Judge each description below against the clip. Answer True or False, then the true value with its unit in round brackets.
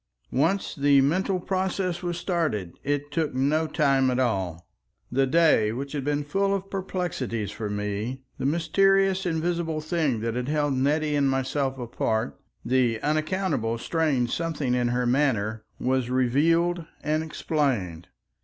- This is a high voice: False (145 Hz)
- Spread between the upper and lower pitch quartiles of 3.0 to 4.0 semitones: False (5.1 semitones)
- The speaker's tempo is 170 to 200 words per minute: False (145 wpm)